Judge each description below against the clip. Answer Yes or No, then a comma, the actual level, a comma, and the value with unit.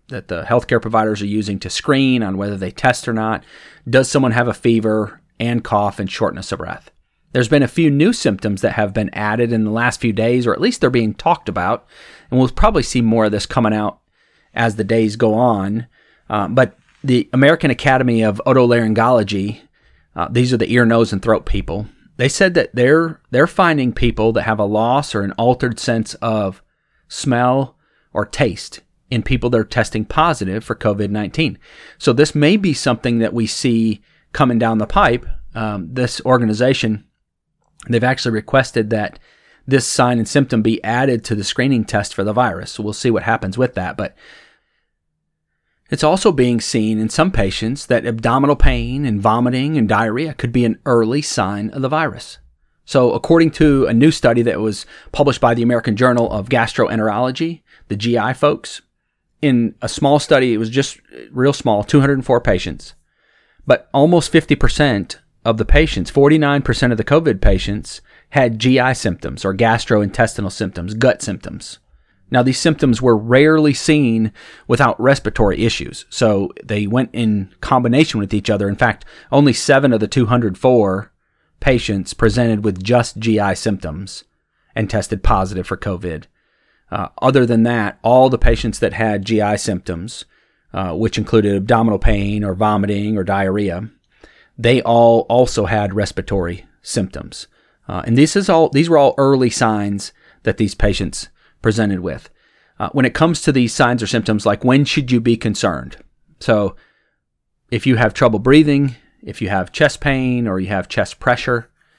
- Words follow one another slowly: No, average, 175 wpm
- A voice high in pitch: No, low, 115 Hz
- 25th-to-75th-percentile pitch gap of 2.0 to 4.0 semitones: Yes, average, 3.5 semitones